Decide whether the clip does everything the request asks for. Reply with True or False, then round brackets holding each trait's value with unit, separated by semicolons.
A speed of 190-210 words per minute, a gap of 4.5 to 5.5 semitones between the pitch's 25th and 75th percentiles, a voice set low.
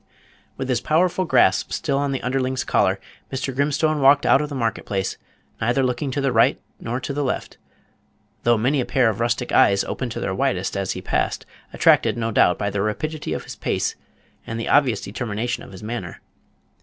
False (195 wpm; 3.7 semitones; 125 Hz)